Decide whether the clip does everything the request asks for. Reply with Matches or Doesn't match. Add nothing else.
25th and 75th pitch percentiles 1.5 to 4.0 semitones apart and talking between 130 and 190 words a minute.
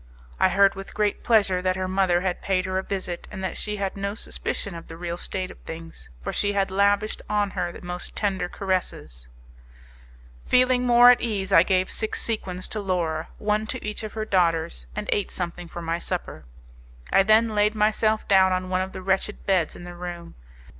Doesn't match